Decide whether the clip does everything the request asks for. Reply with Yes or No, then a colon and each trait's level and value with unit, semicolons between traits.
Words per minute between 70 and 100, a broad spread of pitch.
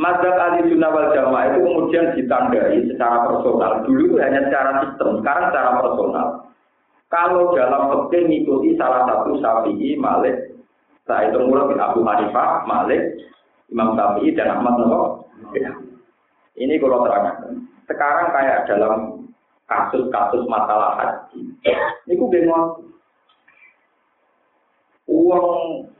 No: average, 115 wpm; wide, 7.3 semitones